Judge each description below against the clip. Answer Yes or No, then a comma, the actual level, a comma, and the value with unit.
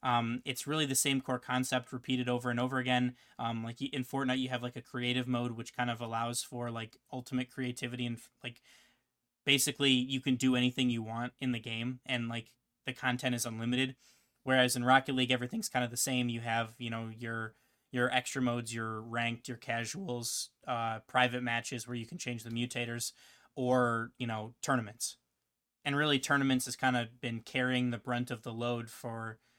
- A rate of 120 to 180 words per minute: No, average, 195 wpm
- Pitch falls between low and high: No, low, 125 Hz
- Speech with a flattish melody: Yes, narrow, 1.5 semitones